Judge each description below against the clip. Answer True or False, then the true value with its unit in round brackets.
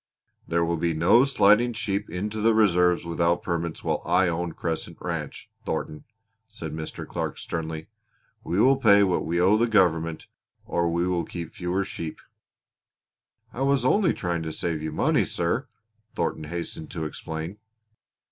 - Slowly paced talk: False (155 wpm)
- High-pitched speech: False (85 Hz)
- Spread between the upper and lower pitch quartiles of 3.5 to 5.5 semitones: True (4.0 semitones)